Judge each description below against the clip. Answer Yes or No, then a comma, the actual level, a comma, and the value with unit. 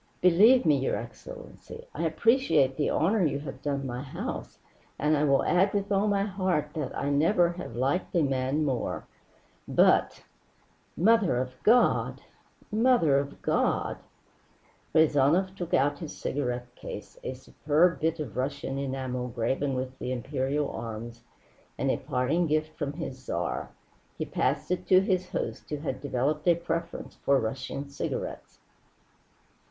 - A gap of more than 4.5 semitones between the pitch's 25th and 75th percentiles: Yes, average, 5.0 semitones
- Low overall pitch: No, medium, 150 Hz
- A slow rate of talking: No, average, 150 wpm